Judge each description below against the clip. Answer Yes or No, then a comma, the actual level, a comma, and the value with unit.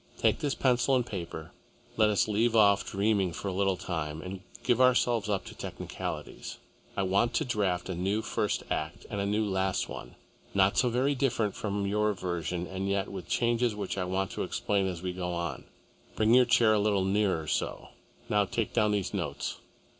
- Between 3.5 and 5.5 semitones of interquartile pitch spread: No, average, 2.9 semitones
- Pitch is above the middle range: No, low, 100 Hz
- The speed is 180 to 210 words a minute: Yes, average, 195 wpm